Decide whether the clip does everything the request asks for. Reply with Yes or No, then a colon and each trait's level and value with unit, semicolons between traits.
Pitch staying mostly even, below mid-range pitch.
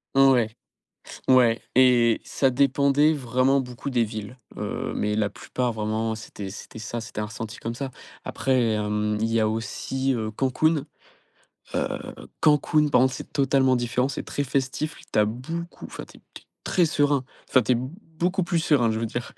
No: average, 3.7 semitones; low, 125 Hz